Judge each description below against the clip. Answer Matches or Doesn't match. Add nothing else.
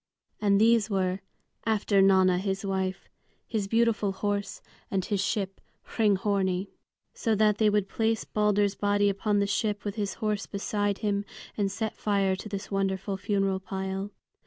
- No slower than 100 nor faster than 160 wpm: Matches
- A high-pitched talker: Matches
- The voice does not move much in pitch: Matches